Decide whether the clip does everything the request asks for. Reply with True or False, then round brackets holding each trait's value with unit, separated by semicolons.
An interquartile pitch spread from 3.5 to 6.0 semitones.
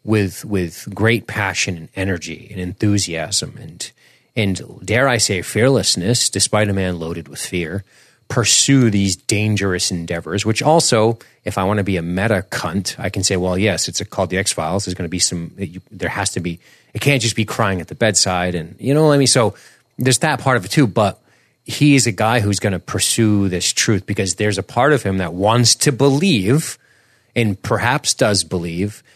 True (4.3 semitones)